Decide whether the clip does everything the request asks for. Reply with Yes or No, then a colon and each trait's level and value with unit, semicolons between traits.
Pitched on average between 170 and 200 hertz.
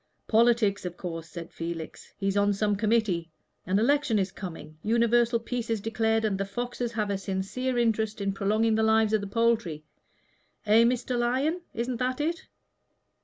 No: high, 220 Hz